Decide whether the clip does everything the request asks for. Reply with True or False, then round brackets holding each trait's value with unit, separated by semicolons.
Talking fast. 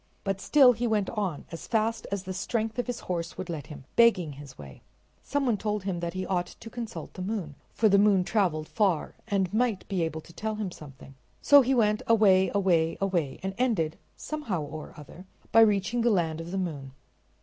True (210 wpm)